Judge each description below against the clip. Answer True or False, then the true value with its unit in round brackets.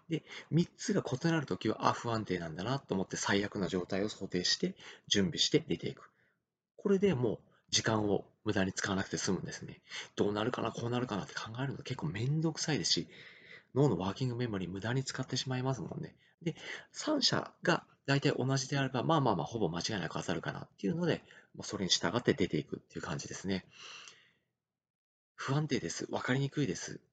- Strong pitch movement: True (6.5 semitones)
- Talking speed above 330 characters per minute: True (405 characters per minute)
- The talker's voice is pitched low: True (125 Hz)